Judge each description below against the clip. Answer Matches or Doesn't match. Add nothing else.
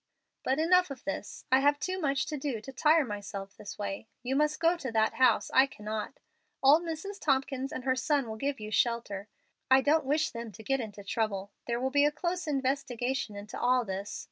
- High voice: Matches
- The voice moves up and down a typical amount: Matches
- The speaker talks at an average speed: Doesn't match